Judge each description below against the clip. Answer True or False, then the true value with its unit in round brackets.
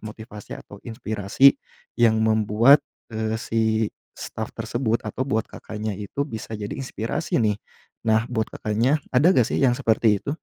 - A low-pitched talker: True (110 Hz)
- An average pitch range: False (2.2 semitones)